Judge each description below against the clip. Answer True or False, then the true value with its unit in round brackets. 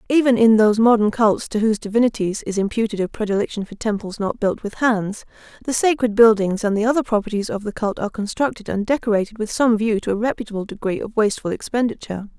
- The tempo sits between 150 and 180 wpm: False (205 wpm)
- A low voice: False (215 Hz)